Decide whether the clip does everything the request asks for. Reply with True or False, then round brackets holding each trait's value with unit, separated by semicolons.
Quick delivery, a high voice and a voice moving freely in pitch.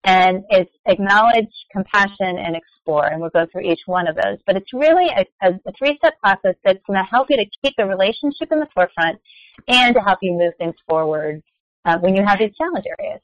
True (215 wpm; 195 Hz; 5.7 semitones)